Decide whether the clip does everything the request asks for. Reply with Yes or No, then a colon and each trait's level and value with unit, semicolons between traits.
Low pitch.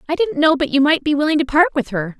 No: very high, 295 Hz